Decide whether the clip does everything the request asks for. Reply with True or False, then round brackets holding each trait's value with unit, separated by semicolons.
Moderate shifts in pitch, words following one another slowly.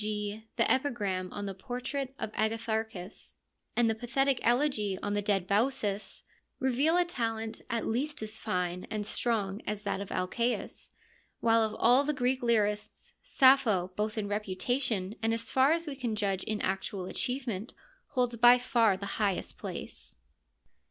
False (3.4 semitones; 160 wpm)